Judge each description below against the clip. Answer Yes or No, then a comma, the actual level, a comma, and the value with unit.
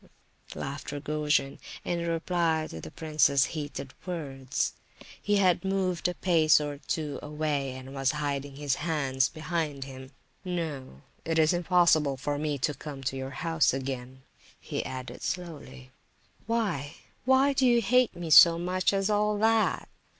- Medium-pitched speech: Yes, medium, 155 Hz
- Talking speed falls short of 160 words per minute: Yes, average, 145 wpm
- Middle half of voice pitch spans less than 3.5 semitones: No, average, 4.4 semitones